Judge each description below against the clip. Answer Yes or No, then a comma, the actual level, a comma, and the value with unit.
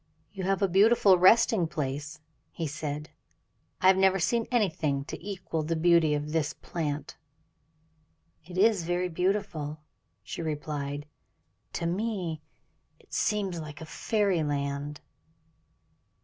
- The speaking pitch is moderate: Yes, medium, 165 Hz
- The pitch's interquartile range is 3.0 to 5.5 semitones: Yes, average, 4.3 semitones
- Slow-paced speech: Yes, slow, 120 wpm